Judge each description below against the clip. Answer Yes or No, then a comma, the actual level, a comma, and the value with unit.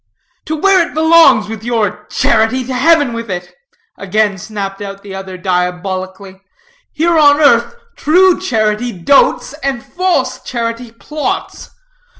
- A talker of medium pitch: No, high, 230 Hz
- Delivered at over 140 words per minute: No, slow, 135 wpm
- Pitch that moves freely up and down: Yes, wide, 6.9 semitones